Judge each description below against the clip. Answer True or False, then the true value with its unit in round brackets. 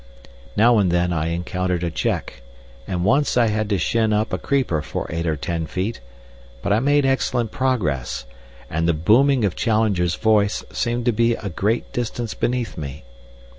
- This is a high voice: False (105 Hz)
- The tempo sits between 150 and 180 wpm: True (175 wpm)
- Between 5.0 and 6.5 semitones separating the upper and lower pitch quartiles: True (5.6 semitones)